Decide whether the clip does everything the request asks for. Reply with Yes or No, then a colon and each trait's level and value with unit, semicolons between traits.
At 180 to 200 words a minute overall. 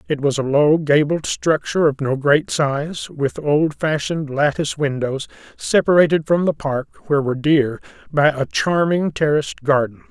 No: average, 155 wpm